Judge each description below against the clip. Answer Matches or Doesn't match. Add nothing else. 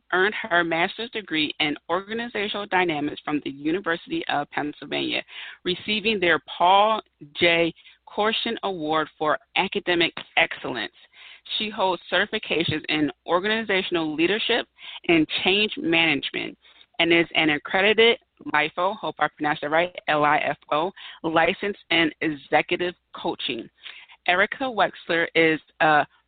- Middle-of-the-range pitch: Matches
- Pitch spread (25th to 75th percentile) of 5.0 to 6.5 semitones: Matches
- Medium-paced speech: Doesn't match